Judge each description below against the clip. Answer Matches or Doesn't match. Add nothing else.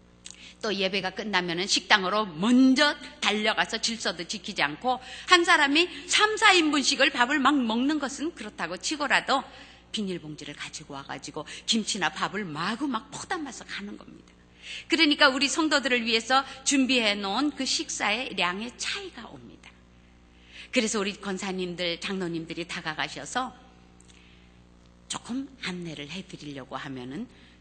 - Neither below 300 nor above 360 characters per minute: Matches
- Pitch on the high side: Matches